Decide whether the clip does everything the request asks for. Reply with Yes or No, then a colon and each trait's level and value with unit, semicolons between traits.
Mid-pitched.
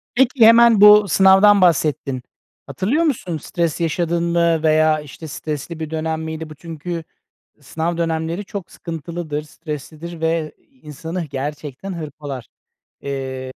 Yes: medium, 160 Hz